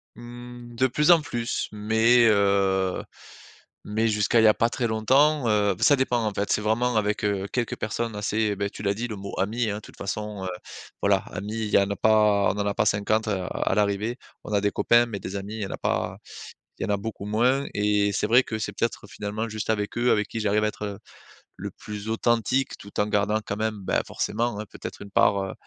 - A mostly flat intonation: Yes, narrow, 2.3 semitones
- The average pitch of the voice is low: Yes, low, 105 Hz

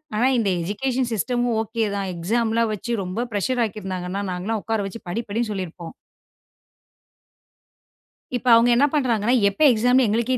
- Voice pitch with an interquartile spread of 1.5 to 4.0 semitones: Yes, average, 3.4 semitones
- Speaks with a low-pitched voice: No, high, 220 Hz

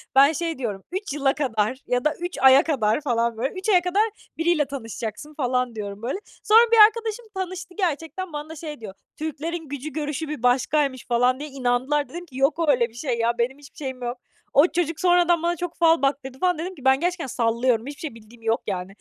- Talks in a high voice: Yes, very high, 285 Hz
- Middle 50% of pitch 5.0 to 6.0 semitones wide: Yes, average, 5.3 semitones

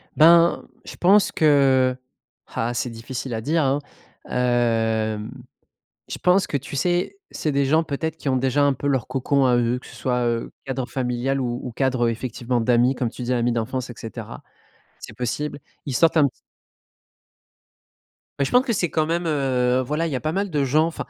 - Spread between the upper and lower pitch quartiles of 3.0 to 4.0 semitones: Yes, average, 3.7 semitones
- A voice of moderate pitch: No, low, 130 Hz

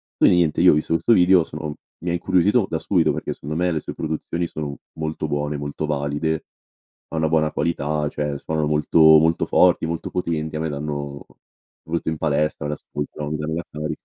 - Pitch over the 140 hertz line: No, very low, 80 Hz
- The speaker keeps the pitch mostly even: Yes, narrow, 1.9 semitones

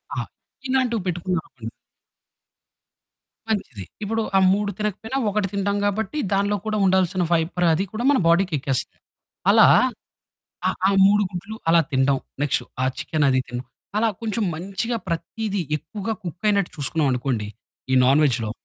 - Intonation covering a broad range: Yes, wide, 5.8 semitones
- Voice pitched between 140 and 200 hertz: Yes, high, 190 Hz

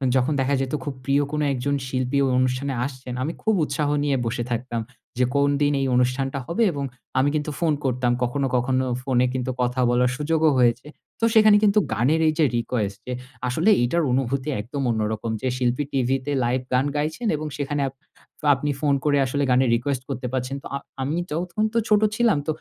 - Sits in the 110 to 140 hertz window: Yes, low, 135 Hz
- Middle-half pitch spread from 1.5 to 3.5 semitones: Yes, average, 2.9 semitones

